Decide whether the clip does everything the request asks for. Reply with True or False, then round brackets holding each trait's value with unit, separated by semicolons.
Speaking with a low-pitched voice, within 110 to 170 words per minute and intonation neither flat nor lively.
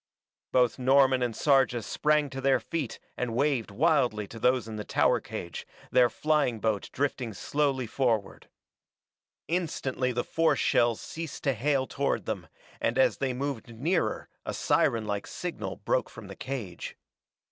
True (130 Hz; 150 wpm; 3.6 semitones)